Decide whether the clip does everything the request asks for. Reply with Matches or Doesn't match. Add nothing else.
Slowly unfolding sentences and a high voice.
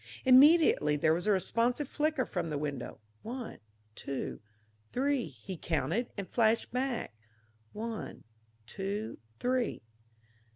Matches